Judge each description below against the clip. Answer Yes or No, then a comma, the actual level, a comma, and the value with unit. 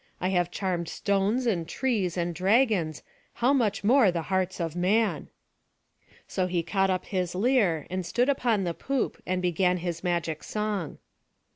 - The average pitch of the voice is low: No, medium, 185 Hz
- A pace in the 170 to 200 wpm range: No, average, 160 wpm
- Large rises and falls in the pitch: No, average, 3.7 semitones